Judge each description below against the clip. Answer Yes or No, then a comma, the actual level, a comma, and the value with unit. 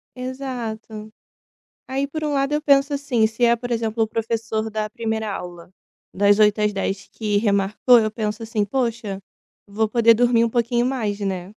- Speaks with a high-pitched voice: Yes, high, 225 Hz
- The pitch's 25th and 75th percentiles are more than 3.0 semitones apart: No, narrow, 2.6 semitones